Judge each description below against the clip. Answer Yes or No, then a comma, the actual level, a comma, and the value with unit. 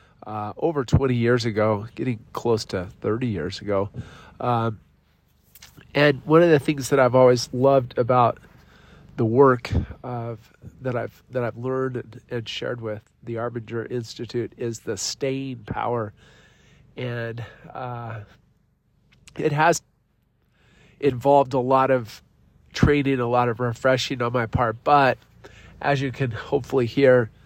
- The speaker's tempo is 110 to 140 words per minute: Yes, slow, 135 wpm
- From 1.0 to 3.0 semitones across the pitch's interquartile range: Yes, narrow, 2.6 semitones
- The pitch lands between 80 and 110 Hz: No, low, 120 Hz